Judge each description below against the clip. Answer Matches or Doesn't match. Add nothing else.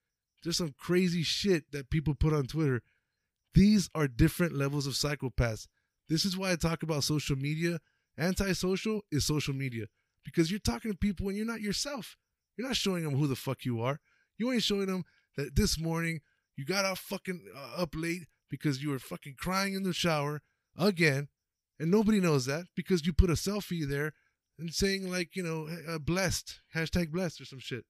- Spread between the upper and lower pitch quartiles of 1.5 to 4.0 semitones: Doesn't match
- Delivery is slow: Doesn't match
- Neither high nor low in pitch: Matches